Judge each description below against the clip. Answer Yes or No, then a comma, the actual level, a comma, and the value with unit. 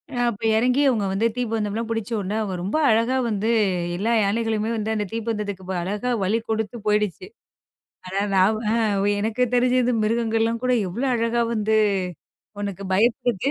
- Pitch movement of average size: No, narrow, 2.2 semitones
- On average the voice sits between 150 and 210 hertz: No, high, 220 Hz